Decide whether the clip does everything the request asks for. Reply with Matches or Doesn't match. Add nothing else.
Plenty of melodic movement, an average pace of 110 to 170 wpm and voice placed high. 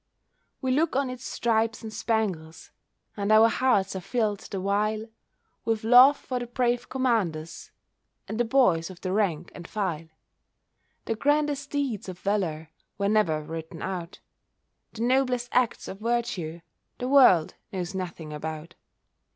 Matches